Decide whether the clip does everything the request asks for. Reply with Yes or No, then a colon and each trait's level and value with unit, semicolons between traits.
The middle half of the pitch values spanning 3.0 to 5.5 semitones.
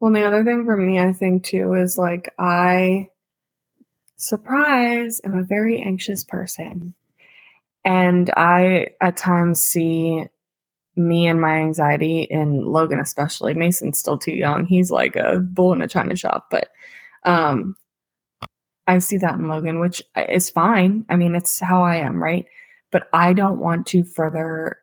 No: narrow, 2.5 semitones